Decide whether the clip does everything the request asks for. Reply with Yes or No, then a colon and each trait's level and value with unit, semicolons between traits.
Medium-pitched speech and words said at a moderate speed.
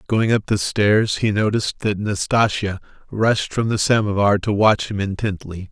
No: low, 105 Hz; average, 170 wpm